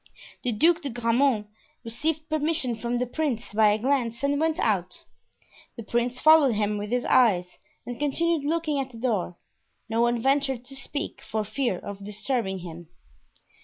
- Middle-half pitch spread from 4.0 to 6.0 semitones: Yes, average, 4.6 semitones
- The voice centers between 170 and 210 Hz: No, high, 245 Hz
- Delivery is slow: No, average, 165 wpm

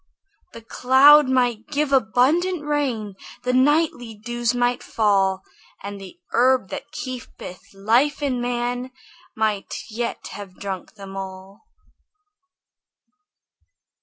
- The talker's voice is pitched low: No, high, 240 Hz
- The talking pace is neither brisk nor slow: No, slow, 105 wpm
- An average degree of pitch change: Yes, average, 4.2 semitones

